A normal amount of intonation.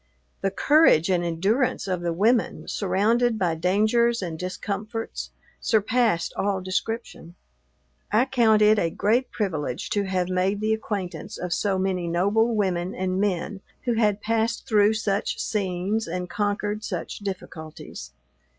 Yes: average, 3.3 semitones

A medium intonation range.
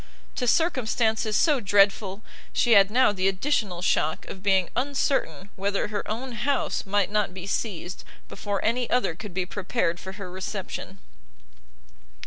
Yes: average, 3.6 semitones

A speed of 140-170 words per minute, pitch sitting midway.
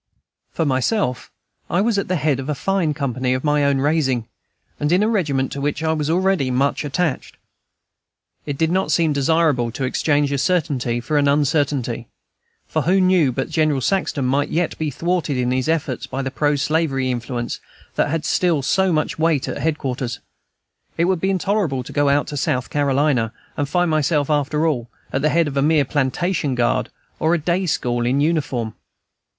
No: average, 190 wpm; medium, 145 Hz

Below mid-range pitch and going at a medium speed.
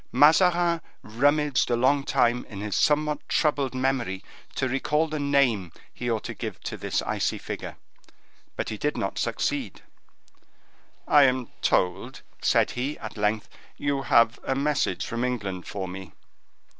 Yes: low, 130 Hz; average, 150 wpm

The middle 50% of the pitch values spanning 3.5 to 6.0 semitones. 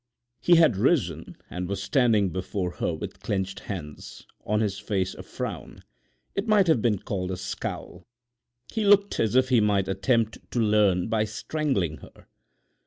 Yes: average, 5.1 semitones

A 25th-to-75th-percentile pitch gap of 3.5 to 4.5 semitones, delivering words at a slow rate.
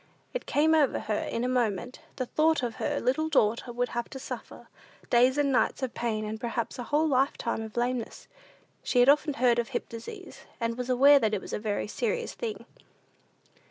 No: average, 3.8 semitones; fast, 205 wpm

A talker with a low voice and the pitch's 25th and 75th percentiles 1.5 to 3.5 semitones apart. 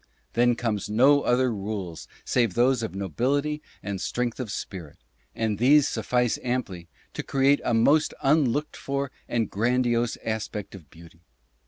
No: low, 120 Hz; average, 4.1 semitones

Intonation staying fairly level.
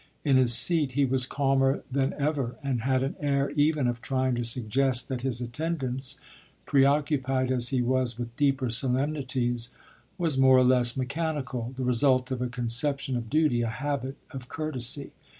Yes: narrow, 2.2 semitones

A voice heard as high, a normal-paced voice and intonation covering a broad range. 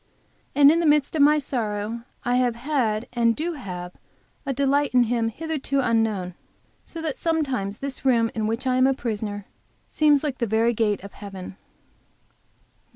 No: high, 245 Hz; average, 170 wpm; average, 4.5 semitones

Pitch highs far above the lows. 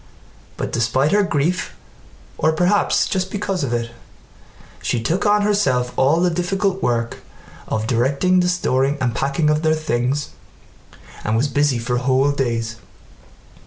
Yes: wide, 6.5 semitones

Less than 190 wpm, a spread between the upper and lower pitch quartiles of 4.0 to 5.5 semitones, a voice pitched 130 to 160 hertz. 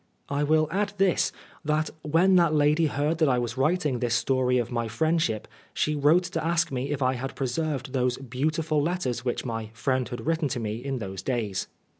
No: average, 200 wpm; average, 4.3 semitones; medium, 140 Hz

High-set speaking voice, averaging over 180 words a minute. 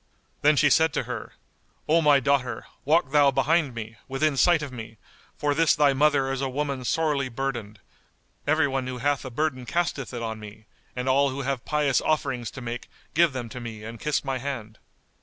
No: low, 135 Hz; average, 195 wpm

